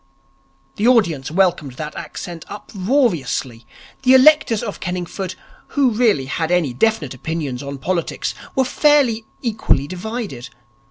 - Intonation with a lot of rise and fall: Yes, wide, 7.6 semitones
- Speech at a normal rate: No, slow, 120 wpm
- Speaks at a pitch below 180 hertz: No, medium, 185 Hz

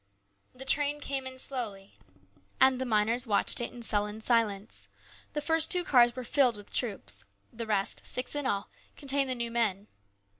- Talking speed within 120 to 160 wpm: No, average, 175 wpm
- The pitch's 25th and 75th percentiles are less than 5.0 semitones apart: Yes, average, 4.1 semitones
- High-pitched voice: Yes, high, 240 Hz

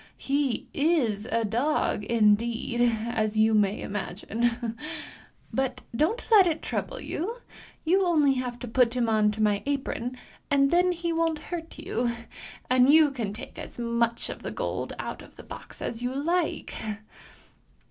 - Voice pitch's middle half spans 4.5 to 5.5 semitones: Yes, average, 5.1 semitones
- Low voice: No, high, 245 Hz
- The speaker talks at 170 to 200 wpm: No, average, 150 wpm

